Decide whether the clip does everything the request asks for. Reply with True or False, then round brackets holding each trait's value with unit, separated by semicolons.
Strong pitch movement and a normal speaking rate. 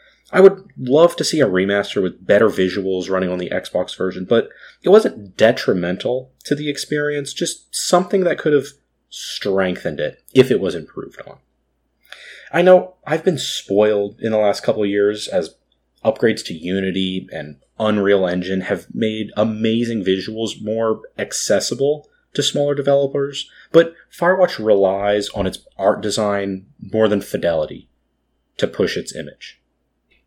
True (7.2 semitones; 150 wpm)